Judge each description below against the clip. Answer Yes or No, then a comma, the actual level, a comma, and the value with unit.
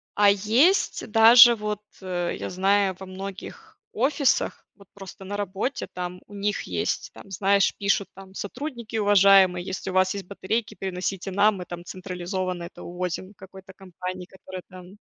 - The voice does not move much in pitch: Yes, narrow, 1.9 semitones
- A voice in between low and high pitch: No, high, 195 Hz